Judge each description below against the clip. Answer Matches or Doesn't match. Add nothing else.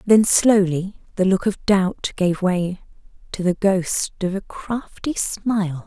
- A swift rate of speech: Doesn't match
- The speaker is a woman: Matches